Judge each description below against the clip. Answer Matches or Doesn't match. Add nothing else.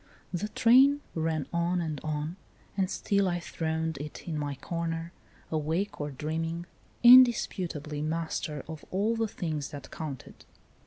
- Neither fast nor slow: Matches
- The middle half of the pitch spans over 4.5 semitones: Doesn't match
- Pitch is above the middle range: Doesn't match